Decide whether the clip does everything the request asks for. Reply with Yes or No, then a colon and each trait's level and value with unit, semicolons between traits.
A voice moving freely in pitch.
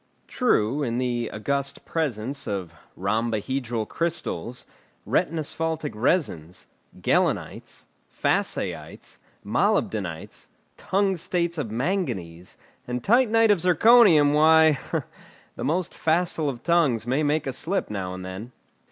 Yes: wide, 7.1 semitones